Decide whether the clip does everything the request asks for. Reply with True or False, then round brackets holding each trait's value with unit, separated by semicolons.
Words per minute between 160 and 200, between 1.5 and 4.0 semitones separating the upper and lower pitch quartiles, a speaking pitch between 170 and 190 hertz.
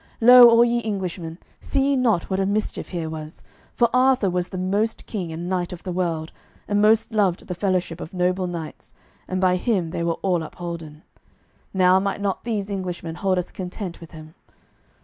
True (190 wpm; 3.3 semitones; 185 Hz)